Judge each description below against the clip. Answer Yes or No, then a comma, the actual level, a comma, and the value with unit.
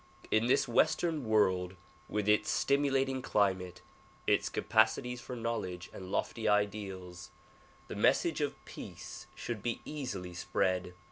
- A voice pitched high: No, low, 105 Hz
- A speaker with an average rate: No, slow, 125 wpm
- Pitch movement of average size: Yes, average, 5.0 semitones